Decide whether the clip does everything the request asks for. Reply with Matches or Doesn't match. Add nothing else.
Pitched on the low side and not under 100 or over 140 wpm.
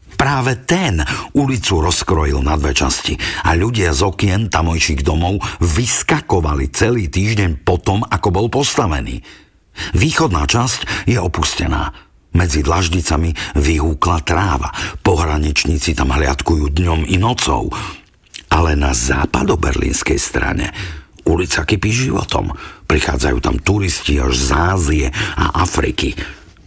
Matches